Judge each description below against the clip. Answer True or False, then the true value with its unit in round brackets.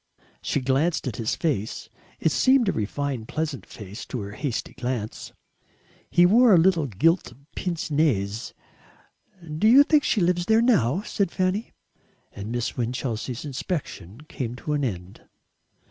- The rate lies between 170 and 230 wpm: False (145 wpm)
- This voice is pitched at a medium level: True (145 Hz)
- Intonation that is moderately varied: False (7.5 semitones)